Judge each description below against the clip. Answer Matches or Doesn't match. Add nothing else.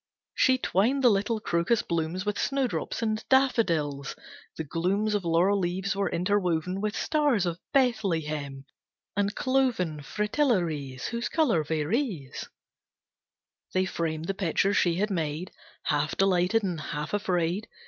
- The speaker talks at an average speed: Doesn't match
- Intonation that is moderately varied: Matches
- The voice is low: Doesn't match